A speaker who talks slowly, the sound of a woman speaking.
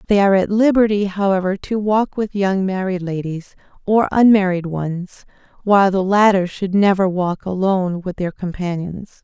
No: average, 155 wpm; female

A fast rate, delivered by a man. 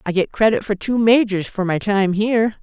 No: fast, 230 wpm; female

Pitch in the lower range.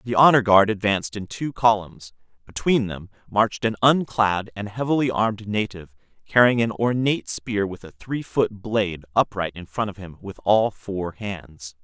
Yes: low, 105 Hz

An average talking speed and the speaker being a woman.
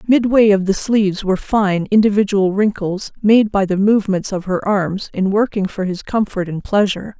Yes: average, 185 wpm; female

